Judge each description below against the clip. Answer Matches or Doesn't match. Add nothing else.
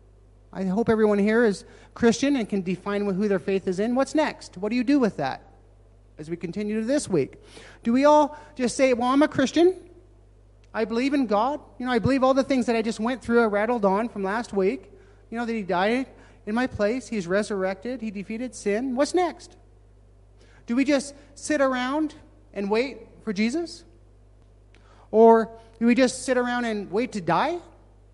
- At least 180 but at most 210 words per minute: Matches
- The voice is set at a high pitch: Matches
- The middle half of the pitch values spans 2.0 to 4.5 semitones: Doesn't match